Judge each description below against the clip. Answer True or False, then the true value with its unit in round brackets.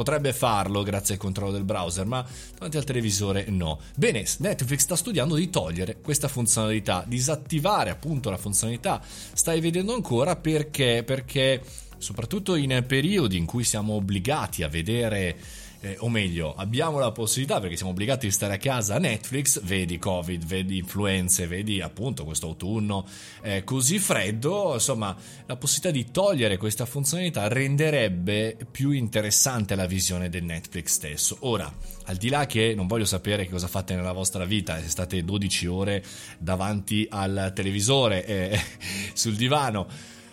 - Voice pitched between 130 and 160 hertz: False (105 Hz)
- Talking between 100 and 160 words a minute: True (150 wpm)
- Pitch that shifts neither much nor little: False (5.8 semitones)